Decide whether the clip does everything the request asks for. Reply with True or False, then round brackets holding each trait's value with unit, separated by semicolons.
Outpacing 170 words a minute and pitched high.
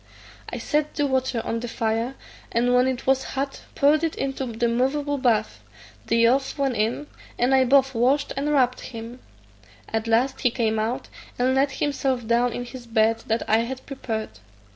True (185 wpm; 250 Hz)